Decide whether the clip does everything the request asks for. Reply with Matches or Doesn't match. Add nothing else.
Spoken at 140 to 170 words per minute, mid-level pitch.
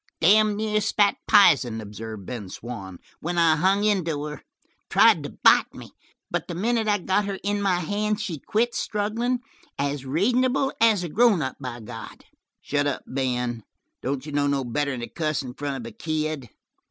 Doesn't match